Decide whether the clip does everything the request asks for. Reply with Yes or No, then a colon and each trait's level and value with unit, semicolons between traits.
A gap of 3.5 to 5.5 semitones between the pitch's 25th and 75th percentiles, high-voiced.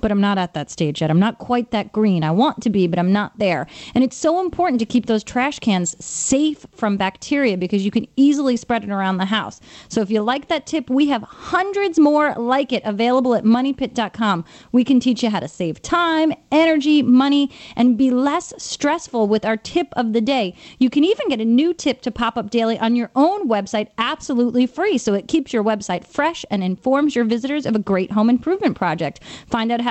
Yes: average, 4.9 semitones; high, 240 Hz